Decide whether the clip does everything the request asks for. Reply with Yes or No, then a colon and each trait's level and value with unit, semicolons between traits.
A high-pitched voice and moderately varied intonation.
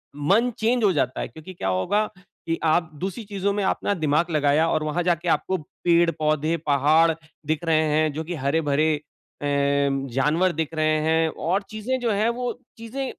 No: medium, 160 Hz; average, 4.2 semitones